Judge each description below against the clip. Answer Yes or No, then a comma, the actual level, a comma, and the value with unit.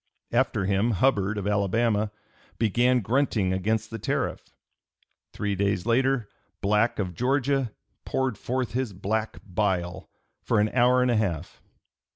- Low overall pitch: Yes, low, 110 Hz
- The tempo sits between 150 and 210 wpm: No, slow, 135 wpm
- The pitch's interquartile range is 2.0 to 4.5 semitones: Yes, average, 3.8 semitones